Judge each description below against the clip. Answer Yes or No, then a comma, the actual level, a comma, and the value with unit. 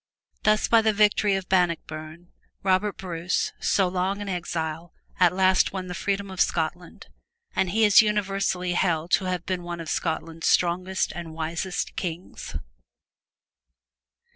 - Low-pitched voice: No, medium, 180 Hz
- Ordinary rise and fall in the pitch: No, narrow, 2.2 semitones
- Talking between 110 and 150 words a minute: Yes, average, 140 wpm